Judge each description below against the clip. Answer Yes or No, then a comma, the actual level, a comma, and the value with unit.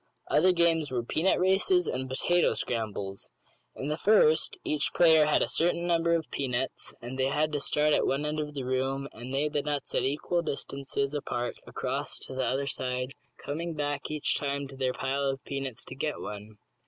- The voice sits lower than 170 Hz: Yes, medium, 140 Hz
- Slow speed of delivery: No, average, 195 wpm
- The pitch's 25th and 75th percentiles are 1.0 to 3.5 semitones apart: Yes, average, 2.8 semitones